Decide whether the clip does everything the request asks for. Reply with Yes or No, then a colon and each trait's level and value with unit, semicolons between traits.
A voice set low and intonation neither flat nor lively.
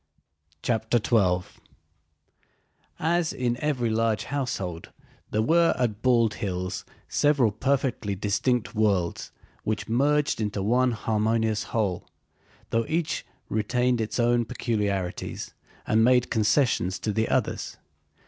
Yes: low, 115 Hz; average, 3.2 semitones